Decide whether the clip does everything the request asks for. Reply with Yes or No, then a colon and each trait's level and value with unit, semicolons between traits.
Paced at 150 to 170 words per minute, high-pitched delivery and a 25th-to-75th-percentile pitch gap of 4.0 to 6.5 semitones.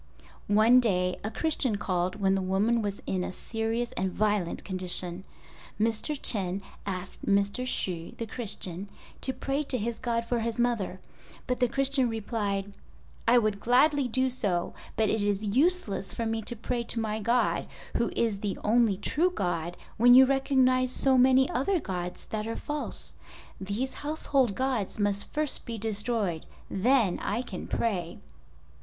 Yes: average, 160 wpm; high, 225 Hz; average, 4.3 semitones